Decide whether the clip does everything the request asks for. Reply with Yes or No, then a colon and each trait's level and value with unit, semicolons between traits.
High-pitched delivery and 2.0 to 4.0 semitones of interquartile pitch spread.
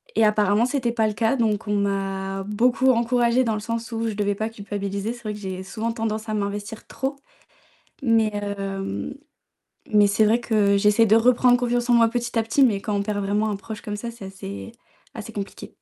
Yes: high, 215 Hz; narrow, 2.4 semitones